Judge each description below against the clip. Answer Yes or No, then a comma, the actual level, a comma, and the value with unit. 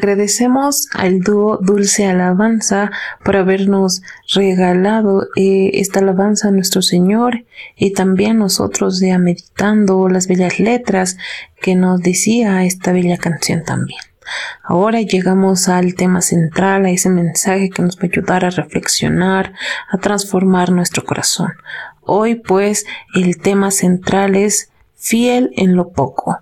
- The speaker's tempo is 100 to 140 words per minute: Yes, average, 130 wpm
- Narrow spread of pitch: Yes, narrow, 1.8 semitones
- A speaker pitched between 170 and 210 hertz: Yes, high, 190 Hz